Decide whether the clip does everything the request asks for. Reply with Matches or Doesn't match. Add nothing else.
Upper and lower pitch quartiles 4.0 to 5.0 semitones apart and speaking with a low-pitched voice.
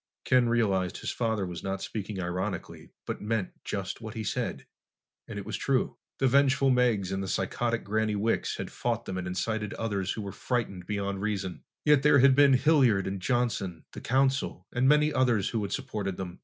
Matches